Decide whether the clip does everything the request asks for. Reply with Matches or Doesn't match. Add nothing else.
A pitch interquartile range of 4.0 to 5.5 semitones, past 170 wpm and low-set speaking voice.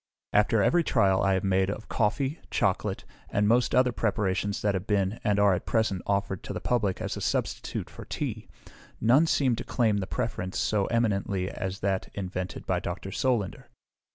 Doesn't match